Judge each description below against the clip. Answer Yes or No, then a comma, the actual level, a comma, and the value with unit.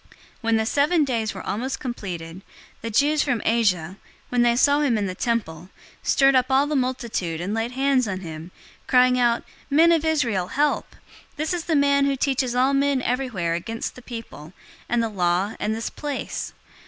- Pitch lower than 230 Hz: No, high, 240 Hz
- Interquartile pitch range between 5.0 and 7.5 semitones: Yes, average, 5.3 semitones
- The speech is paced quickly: No, average, 190 wpm